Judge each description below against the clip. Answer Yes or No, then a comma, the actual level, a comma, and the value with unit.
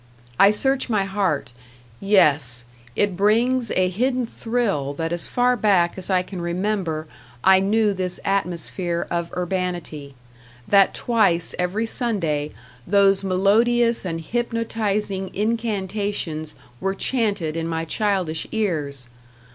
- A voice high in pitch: Yes, high, 195 Hz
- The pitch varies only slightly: No, average, 4.0 semitones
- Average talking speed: No, slow, 120 wpm